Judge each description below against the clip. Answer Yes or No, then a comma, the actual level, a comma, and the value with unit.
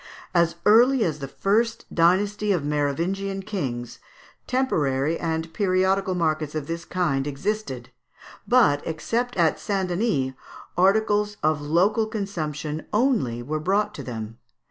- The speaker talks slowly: Yes, slow, 125 wpm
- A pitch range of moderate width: No, wide, 5.8 semitones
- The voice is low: No, medium, 175 Hz